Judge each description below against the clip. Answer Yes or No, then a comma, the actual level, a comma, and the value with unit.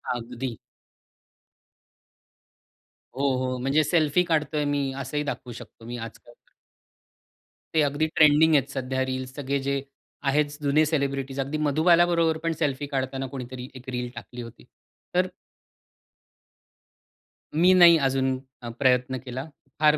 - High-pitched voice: No, low, 135 Hz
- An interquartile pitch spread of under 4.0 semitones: Yes, average, 2.9 semitones